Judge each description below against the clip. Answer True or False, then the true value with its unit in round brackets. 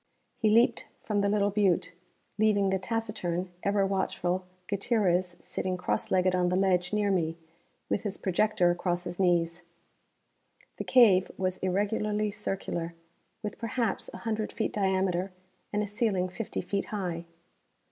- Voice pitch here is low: False (190 Hz)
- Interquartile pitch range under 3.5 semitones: True (2.7 semitones)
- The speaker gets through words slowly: False (145 wpm)